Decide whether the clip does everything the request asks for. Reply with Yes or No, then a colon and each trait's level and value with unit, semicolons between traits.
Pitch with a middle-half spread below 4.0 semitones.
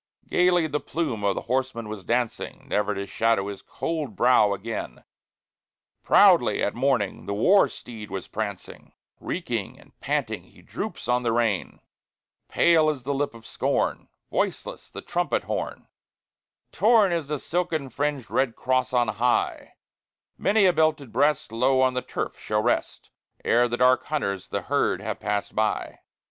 No: wide, 5.4 semitones